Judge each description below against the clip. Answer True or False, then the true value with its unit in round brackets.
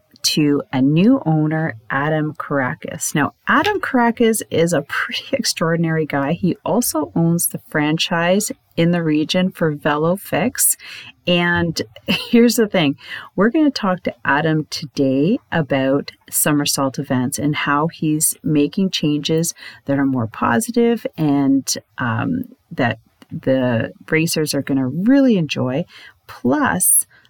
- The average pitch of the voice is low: False (160 Hz)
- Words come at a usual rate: False (125 wpm)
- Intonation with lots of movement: False (4.9 semitones)